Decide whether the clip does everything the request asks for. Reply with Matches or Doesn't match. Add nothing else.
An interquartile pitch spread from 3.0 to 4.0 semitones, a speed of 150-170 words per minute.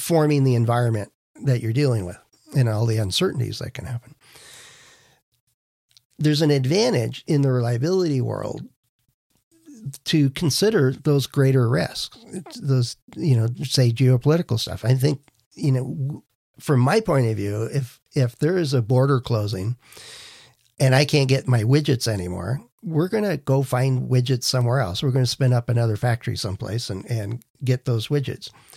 Matches